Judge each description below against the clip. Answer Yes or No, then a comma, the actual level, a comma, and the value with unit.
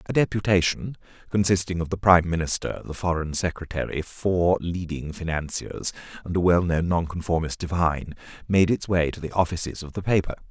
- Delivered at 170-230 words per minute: No, average, 155 wpm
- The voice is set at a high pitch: No, very low, 85 Hz